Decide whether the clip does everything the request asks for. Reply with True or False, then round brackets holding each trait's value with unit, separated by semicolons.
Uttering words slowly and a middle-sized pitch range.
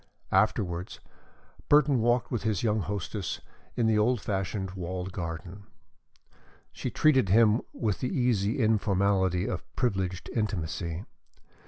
True (120 wpm; 3.6 semitones)